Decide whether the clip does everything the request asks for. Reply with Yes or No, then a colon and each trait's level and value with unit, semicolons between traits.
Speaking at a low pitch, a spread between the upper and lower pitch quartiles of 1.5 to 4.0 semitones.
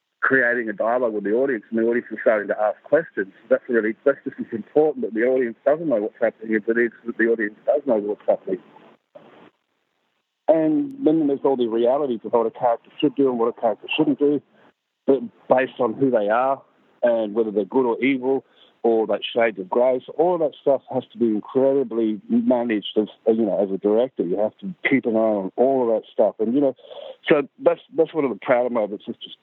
Yes: low, 120 Hz; average, 3.5 semitones